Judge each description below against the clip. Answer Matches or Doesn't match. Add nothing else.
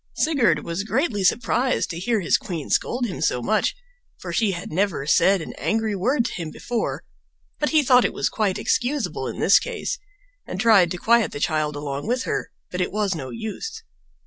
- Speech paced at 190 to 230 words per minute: Matches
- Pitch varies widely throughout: Matches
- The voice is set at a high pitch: Matches